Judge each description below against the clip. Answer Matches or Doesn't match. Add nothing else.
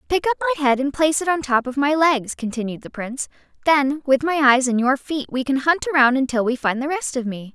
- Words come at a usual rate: Doesn't match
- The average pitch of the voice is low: Doesn't match